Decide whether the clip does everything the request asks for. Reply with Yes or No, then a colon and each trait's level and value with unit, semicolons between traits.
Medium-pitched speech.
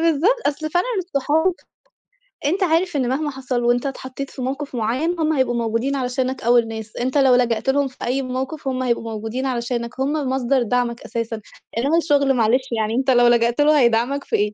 No: very high, 260 Hz